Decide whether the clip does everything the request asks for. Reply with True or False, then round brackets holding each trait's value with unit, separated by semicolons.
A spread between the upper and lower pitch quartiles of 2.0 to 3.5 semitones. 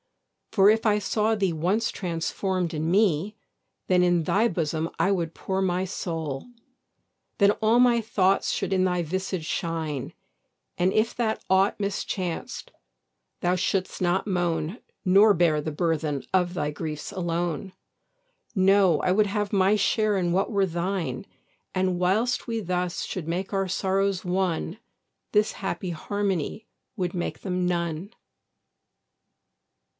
True (2.7 semitones)